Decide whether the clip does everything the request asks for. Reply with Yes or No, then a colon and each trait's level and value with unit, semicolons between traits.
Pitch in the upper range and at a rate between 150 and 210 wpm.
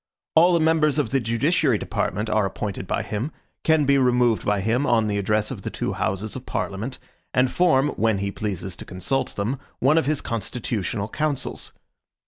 No: low, 115 Hz; average, 185 wpm